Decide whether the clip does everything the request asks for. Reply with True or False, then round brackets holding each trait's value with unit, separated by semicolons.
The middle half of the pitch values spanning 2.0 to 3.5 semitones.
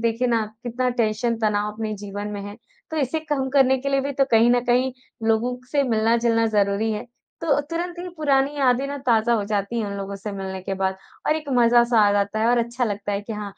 False (4.1 semitones)